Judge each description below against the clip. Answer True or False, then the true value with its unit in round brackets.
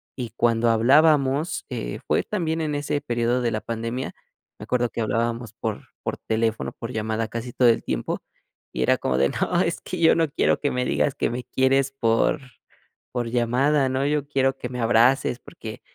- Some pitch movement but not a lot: True (3.1 semitones)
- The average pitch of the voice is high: False (125 Hz)